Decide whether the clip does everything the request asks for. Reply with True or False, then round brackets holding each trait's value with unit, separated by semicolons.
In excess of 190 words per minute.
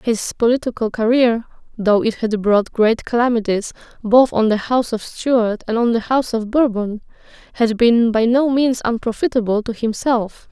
False (165 wpm)